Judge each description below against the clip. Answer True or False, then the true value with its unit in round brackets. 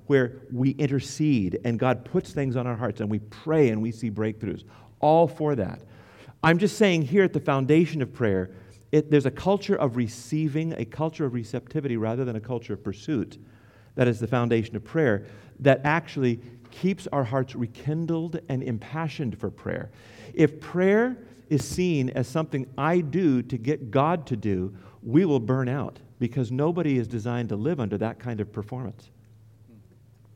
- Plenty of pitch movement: False (4.9 semitones)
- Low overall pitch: True (125 Hz)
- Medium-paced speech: True (175 wpm)